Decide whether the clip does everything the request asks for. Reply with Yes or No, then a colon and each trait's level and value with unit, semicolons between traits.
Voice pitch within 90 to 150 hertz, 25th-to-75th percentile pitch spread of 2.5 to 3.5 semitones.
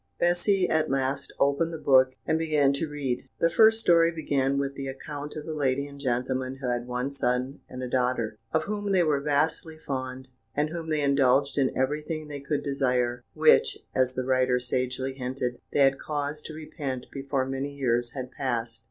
Yes: medium, 140 Hz; average, 2.8 semitones